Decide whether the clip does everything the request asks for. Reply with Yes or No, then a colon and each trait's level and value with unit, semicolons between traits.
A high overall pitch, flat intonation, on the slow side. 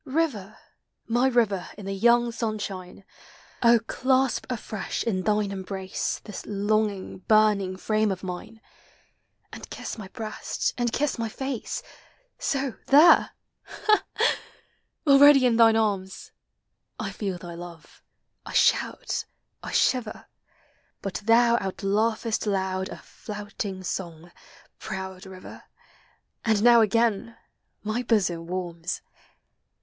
No: high, 215 Hz; average, 3.7 semitones; slow, 125 wpm